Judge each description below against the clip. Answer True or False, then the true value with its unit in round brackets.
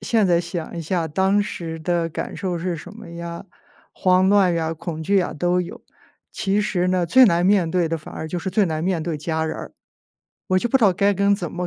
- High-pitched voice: False (175 Hz)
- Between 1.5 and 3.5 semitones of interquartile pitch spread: True (2.7 semitones)